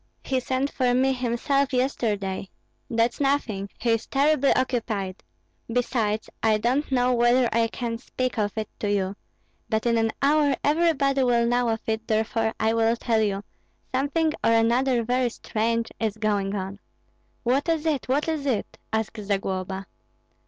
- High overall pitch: Yes, high, 235 Hz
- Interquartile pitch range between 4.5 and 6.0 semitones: No, average, 3.3 semitones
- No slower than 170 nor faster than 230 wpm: No, average, 160 wpm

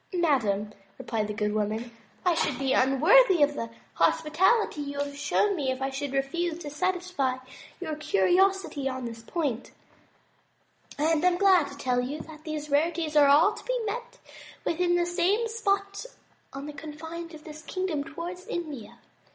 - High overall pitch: Yes, very high, 305 Hz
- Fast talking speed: No, average, 170 wpm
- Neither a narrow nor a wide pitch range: Yes, average, 4.6 semitones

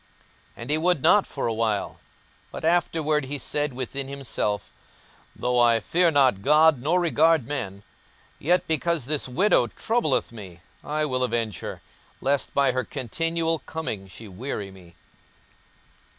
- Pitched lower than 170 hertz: Yes, medium, 140 Hz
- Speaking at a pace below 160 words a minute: Yes, average, 150 wpm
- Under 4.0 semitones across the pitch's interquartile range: No, wide, 5.6 semitones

